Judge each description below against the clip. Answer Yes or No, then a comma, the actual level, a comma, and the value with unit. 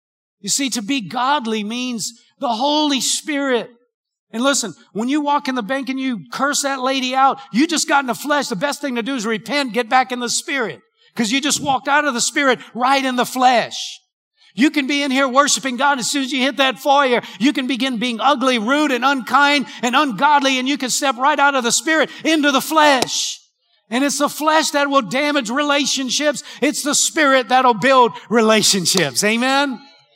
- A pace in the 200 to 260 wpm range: Yes, fast, 205 wpm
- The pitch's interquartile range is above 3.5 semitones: No, average, 2.8 semitones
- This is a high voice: Yes, very high, 270 Hz